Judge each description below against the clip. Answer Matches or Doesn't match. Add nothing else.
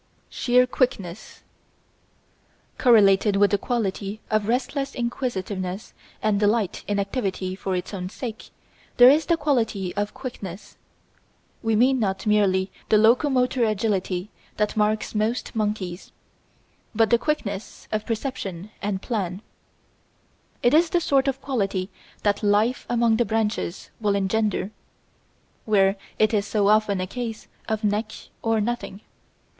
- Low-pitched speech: Doesn't match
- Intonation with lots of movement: Doesn't match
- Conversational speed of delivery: Doesn't match